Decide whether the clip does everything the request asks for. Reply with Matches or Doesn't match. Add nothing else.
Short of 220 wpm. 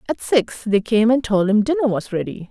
Doesn't match